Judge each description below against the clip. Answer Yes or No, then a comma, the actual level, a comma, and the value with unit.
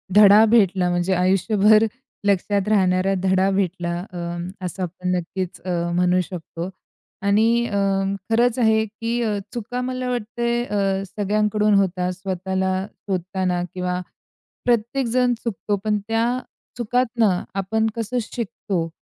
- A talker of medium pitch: No, high, 200 Hz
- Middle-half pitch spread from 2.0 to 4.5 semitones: Yes, average, 3.4 semitones